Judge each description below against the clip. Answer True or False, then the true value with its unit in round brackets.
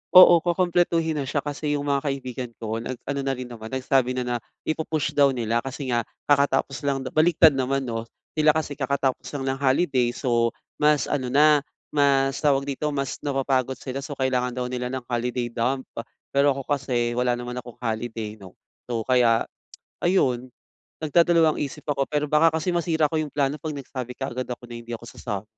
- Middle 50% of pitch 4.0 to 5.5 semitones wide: False (3.0 semitones)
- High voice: False (135 Hz)